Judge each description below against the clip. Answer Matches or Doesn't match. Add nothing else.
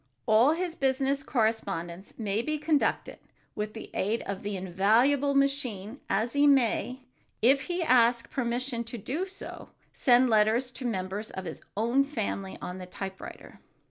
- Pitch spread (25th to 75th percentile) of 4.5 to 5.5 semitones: Matches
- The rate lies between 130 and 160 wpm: Matches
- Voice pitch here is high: Matches